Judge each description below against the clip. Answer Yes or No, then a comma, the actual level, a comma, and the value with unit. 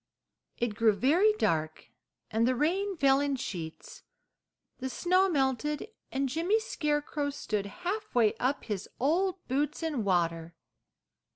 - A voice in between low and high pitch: No, very high, 275 Hz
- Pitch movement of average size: No, wide, 7.2 semitones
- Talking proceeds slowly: Yes, slow, 125 wpm